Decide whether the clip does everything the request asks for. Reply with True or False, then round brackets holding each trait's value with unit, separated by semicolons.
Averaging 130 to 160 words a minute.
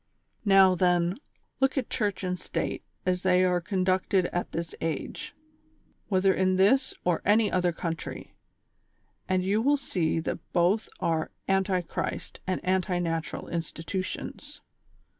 True (140 wpm)